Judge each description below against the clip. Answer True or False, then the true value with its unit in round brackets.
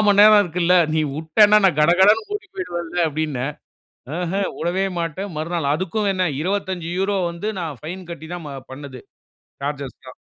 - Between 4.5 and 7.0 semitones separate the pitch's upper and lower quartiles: False (3.4 semitones)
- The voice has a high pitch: False (175 Hz)